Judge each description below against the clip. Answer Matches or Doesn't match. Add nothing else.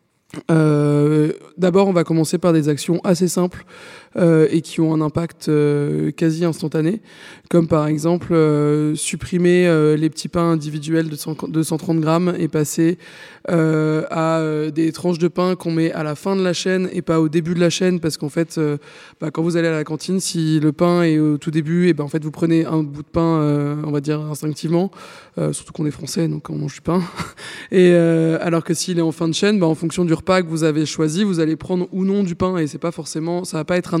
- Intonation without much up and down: Matches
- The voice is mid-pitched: Matches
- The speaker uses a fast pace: Matches